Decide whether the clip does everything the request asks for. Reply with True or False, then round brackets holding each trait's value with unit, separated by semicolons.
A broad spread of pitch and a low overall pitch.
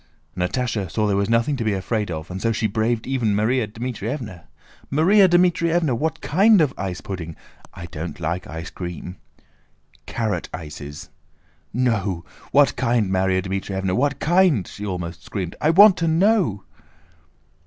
True (7.0 semitones; 110 Hz)